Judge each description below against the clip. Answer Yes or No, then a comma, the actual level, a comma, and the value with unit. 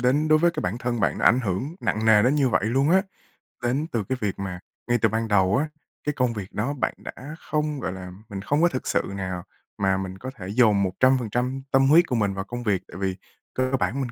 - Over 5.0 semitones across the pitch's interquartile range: Yes, wide, 5.5 semitones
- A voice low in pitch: Yes, low, 120 Hz